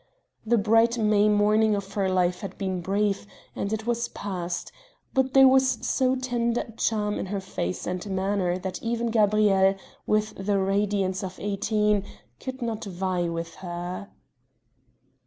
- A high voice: Yes, high, 205 Hz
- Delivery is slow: No, average, 155 wpm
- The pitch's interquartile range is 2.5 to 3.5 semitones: Yes, average, 2.8 semitones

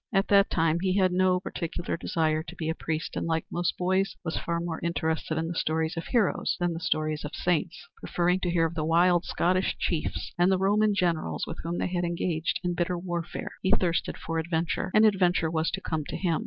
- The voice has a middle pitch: Yes, medium, 175 Hz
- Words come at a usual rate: No, fast, 220 wpm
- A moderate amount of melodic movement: No, narrow, 2.1 semitones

